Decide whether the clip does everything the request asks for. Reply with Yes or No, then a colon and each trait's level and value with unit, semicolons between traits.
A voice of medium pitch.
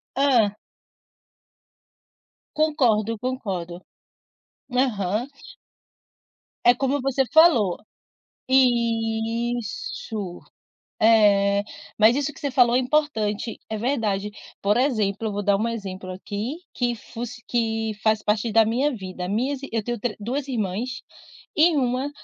No: high, 230 Hz